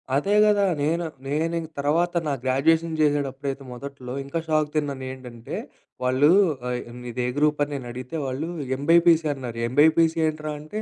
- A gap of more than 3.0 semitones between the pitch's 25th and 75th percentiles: Yes, average, 3.5 semitones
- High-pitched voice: No, medium, 145 Hz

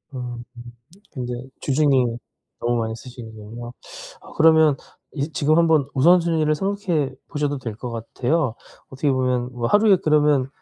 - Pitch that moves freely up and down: No, average, 4.4 semitones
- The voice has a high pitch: No, medium, 140 Hz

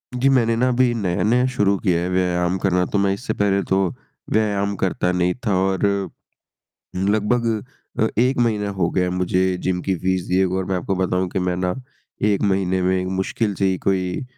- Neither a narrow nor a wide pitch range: No, narrow, 2.3 semitones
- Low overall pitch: Yes, very low, 95 Hz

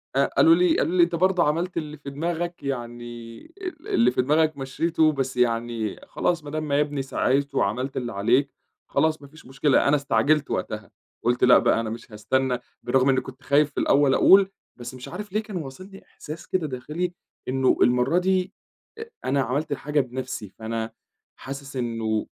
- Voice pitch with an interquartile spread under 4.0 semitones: No, average, 4.3 semitones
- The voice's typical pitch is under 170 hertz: Yes, medium, 140 Hz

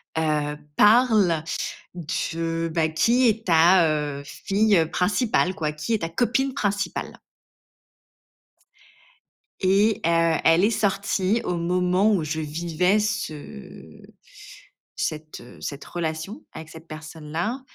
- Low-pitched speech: No, medium, 170 Hz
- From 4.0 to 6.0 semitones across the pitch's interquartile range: Yes, average, 4.6 semitones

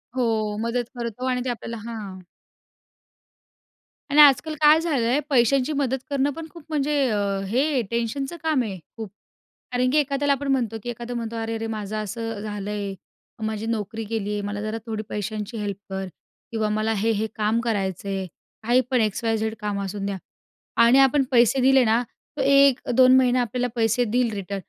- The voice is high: Yes, high, 230 Hz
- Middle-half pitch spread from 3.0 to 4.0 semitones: Yes, average, 3.5 semitones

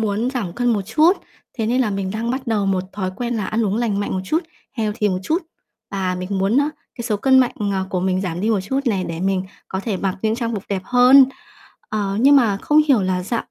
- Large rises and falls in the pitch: No, average, 4.2 semitones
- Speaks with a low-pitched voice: No, high, 210 Hz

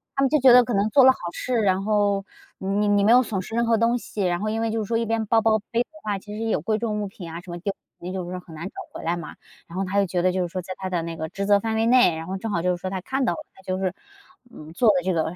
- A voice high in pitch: Yes, high, 200 Hz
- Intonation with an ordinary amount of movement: Yes, average, 3.6 semitones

